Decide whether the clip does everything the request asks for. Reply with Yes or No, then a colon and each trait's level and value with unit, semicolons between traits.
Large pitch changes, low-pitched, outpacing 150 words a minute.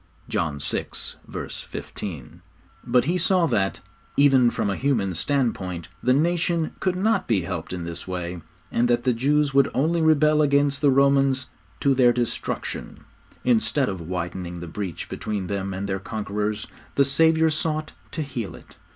Yes: wide, 7.2 semitones; low, 125 Hz; average, 160 wpm